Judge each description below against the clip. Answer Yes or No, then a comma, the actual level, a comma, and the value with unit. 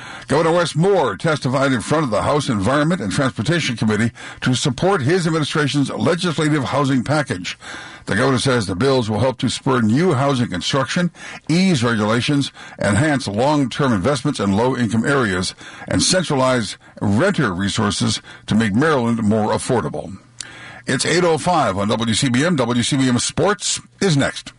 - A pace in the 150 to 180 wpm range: No, average, 140 wpm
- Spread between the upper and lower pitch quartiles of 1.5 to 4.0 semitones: No, average, 4.6 semitones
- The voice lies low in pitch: Yes, low, 130 Hz